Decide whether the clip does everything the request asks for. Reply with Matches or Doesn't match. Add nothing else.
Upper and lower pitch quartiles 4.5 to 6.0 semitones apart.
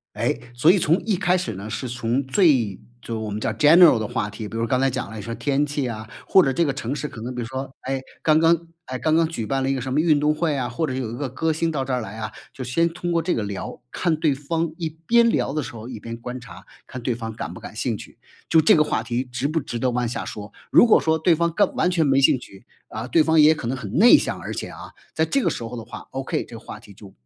Matches